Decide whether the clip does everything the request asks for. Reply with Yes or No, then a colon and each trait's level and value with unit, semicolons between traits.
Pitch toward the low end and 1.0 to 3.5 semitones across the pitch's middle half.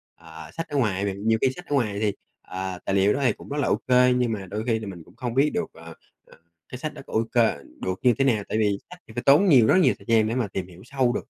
No: low, 115 Hz; average, 4.8 semitones